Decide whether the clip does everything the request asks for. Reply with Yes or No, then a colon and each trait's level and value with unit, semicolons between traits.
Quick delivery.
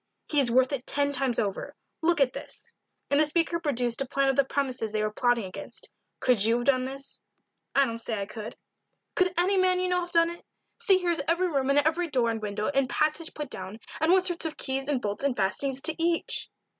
Yes: fast, 235 wpm